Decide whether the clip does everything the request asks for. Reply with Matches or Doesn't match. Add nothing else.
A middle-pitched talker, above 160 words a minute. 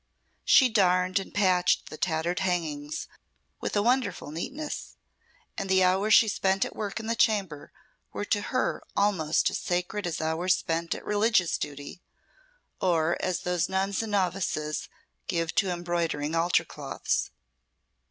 Doesn't match